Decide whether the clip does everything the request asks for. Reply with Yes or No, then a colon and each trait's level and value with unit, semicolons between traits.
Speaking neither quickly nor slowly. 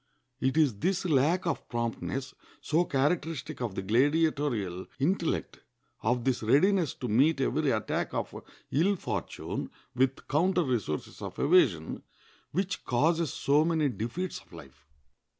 No: slow, 130 wpm